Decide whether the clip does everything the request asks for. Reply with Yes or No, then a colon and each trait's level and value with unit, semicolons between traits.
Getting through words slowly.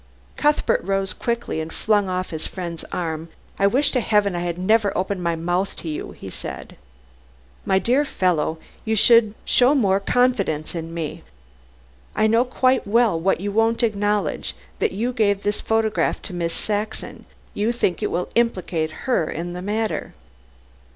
No: average, 165 wpm